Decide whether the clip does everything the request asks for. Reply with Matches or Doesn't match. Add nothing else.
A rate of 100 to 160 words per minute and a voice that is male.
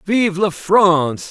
Matches